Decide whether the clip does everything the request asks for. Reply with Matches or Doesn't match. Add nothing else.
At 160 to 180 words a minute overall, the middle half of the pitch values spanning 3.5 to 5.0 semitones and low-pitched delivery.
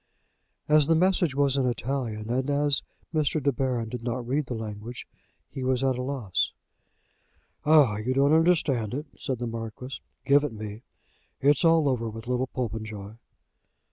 Matches